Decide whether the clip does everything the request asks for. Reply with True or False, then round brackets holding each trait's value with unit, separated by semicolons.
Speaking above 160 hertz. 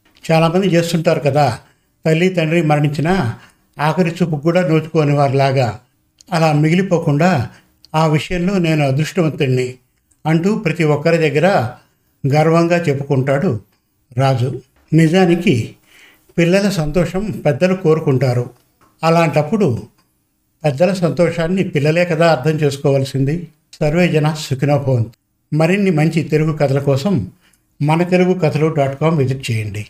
False (155 Hz)